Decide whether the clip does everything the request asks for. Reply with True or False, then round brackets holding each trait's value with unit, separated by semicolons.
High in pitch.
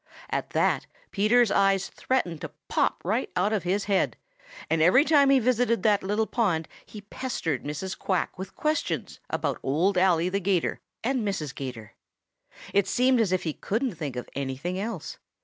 True (195 Hz)